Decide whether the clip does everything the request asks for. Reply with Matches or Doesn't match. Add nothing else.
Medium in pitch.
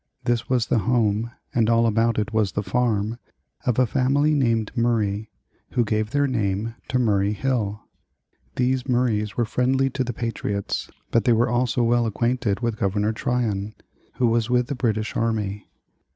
Doesn't match